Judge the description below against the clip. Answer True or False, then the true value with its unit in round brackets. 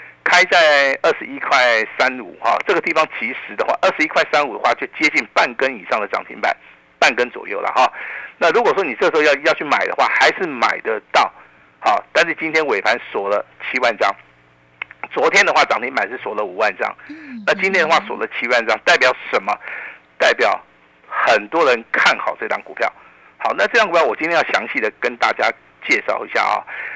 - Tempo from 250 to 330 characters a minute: True (300 characters per minute)